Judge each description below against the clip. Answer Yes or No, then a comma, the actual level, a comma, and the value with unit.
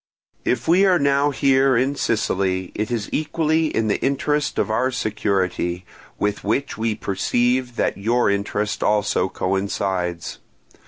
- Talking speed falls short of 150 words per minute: Yes, average, 140 wpm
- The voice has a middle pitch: No, low, 110 Hz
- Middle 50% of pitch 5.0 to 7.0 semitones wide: Yes, average, 5.3 semitones